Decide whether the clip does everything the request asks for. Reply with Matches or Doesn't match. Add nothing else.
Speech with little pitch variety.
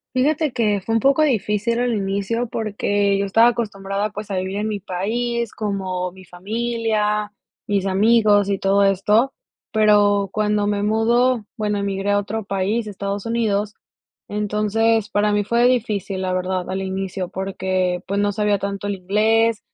Matches